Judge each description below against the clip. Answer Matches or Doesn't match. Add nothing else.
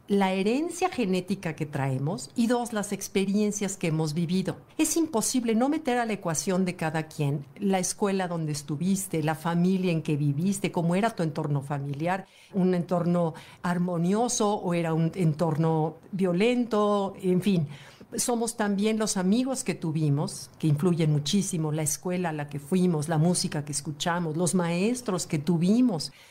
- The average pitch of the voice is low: Doesn't match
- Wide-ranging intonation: Doesn't match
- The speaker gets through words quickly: Doesn't match